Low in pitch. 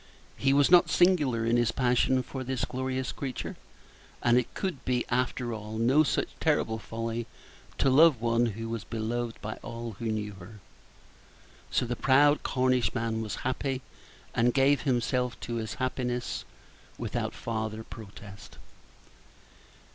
Yes: low, 120 Hz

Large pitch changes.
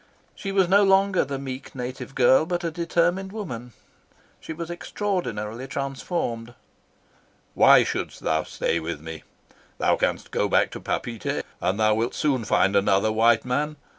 Yes: wide, 7.5 semitones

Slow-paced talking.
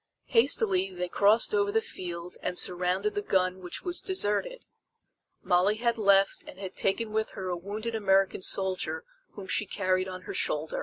No: average, 170 wpm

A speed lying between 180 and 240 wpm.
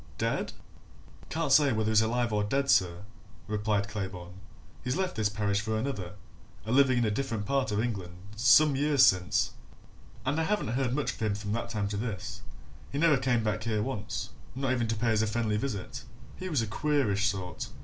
Yes: average, 200 wpm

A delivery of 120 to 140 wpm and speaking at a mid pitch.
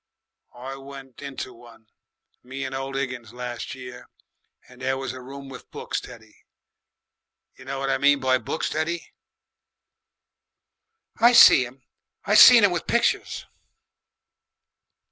No: slow, 135 wpm; low, 130 Hz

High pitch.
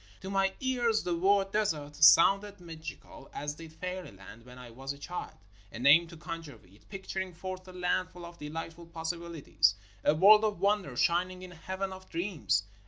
No: medium, 170 Hz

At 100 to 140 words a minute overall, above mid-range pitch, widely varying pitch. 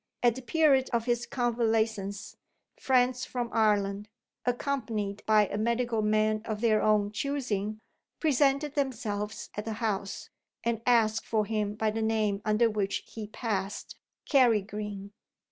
No: slow, 135 wpm; high, 220 Hz; narrow, 2.5 semitones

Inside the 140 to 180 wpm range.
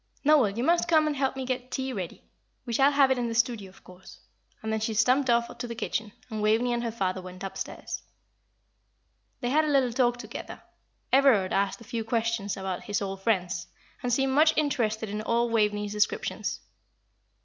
No: average, 195 wpm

